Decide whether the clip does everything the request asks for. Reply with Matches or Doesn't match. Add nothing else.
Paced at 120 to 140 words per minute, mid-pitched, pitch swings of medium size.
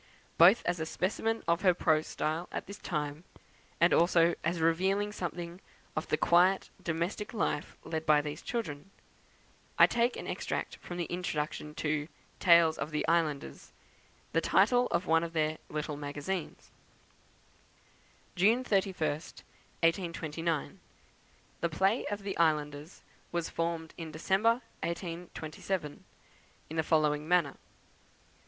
Matches